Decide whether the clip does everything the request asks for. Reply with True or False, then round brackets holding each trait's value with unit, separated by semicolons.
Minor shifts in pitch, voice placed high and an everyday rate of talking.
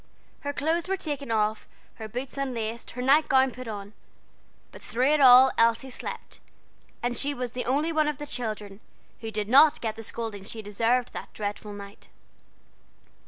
False (4.2 semitones; 245 Hz; 175 wpm)